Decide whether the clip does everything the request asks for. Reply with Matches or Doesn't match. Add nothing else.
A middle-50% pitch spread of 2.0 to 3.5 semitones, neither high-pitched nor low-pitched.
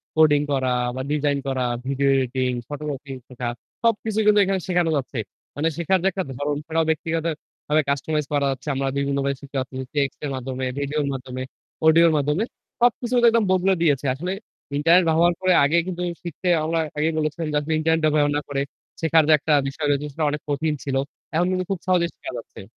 Matches